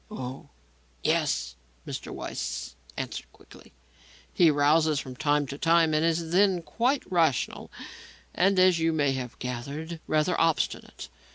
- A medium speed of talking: No, slow, 130 wpm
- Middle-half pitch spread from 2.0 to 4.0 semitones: Yes, average, 3.2 semitones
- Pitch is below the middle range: No, medium, 160 Hz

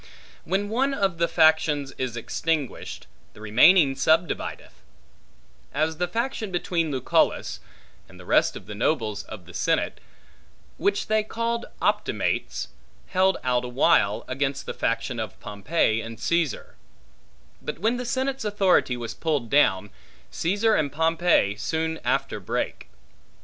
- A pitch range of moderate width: No, wide, 7.8 semitones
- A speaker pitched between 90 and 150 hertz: No, medium, 160 Hz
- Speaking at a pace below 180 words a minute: Yes, slow, 135 wpm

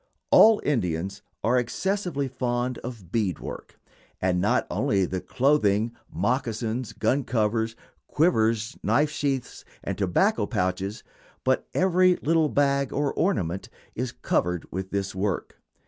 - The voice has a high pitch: No, low, 120 Hz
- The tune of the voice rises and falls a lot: Yes, wide, 6.0 semitones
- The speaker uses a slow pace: Yes, slow, 125 wpm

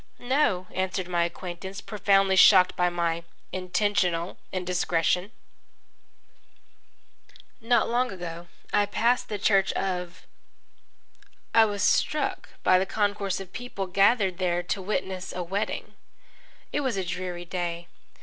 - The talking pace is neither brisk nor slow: No, slow, 120 wpm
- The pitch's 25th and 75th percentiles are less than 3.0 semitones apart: Yes, narrow, 2.4 semitones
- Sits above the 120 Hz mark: Yes, high, 190 Hz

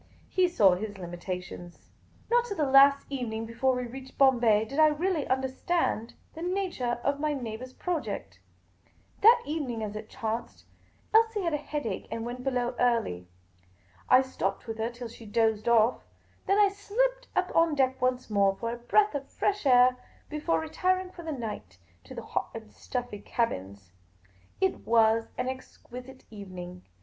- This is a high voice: Yes, very high, 250 Hz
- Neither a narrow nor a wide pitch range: No, wide, 5.7 semitones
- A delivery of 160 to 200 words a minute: Yes, average, 165 wpm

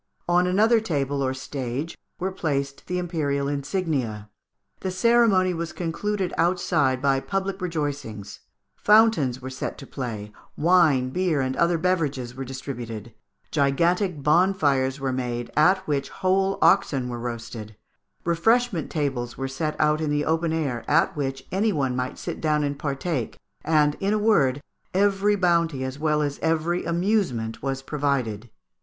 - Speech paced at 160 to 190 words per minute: No, average, 150 wpm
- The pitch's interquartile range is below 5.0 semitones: No, average, 5.3 semitones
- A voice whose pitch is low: No, medium, 150 Hz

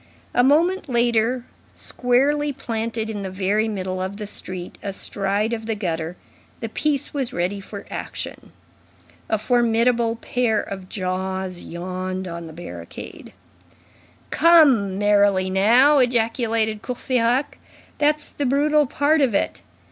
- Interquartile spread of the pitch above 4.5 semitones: Yes, average, 4.9 semitones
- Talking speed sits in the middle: No, slow, 125 wpm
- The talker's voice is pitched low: No, high, 220 Hz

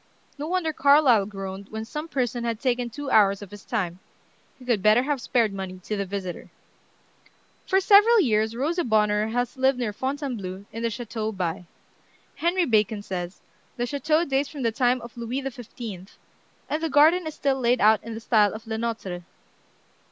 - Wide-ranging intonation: No, average, 4.7 semitones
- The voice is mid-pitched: No, high, 235 Hz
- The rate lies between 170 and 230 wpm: Yes, average, 180 wpm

